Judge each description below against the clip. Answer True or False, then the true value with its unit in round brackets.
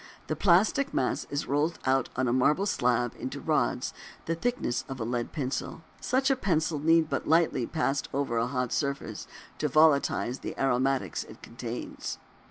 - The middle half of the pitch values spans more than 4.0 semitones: True (4.5 semitones)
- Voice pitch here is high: False (140 Hz)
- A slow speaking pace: False (175 wpm)